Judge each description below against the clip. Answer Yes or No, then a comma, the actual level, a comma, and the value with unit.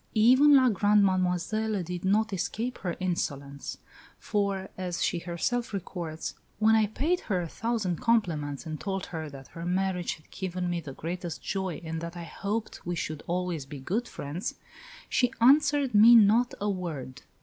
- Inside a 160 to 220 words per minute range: Yes, average, 170 wpm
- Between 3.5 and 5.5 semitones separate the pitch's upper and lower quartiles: Yes, average, 4.5 semitones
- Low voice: No, medium, 185 Hz